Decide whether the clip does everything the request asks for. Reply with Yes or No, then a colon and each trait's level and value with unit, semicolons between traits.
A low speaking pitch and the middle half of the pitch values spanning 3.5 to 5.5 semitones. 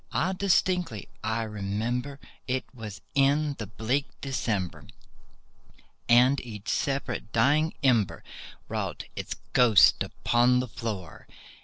Yes: low, 125 Hz; average, 4.2 semitones